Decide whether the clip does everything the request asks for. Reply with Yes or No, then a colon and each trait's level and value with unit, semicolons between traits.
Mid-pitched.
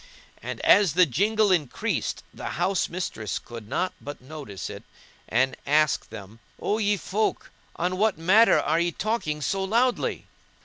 Yes: medium, 175 Hz